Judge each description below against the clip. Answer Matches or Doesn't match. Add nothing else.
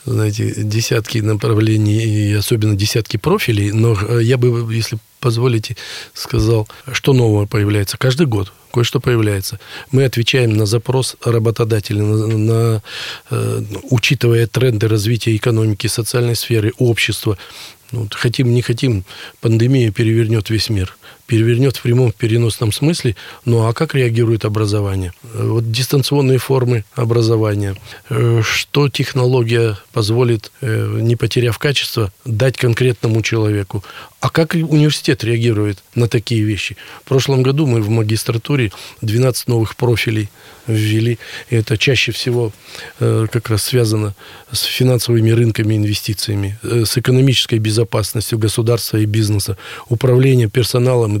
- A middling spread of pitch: Doesn't match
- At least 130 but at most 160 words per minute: Doesn't match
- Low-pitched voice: Matches